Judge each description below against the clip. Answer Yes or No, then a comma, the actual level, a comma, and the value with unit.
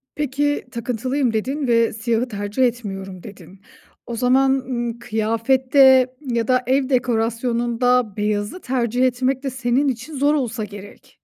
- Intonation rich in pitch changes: No, average, 2.7 semitones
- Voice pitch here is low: No, high, 245 Hz